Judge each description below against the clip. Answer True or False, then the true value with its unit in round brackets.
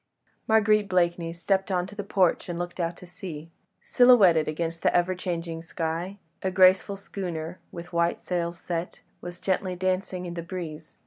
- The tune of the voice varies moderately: False (1.9 semitones)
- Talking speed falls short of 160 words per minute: False (170 wpm)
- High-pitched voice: False (175 Hz)